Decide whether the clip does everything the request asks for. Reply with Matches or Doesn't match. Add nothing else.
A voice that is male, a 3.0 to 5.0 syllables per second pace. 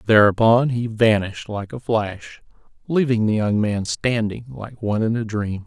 Matches